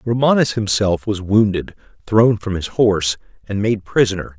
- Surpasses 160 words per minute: No, average, 150 wpm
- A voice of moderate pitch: No, low, 105 Hz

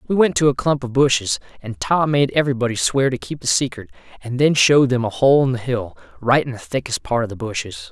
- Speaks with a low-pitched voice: Yes, low, 130 Hz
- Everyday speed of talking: No, fast, 250 wpm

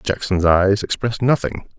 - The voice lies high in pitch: No, low, 105 Hz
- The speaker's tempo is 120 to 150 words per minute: Yes, slow, 135 wpm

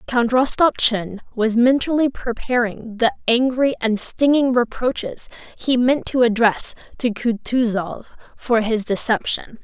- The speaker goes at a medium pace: No, slow, 120 wpm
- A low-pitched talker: No, high, 240 Hz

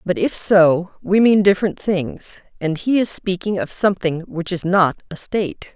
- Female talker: Yes, female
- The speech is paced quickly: No, average, 190 wpm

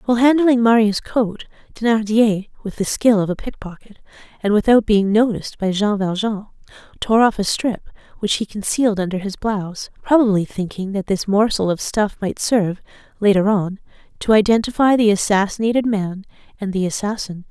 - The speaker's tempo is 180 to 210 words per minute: No, average, 160 wpm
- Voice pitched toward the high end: Yes, high, 210 Hz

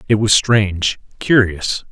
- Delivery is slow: Yes, slow, 125 wpm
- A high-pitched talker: No, low, 105 Hz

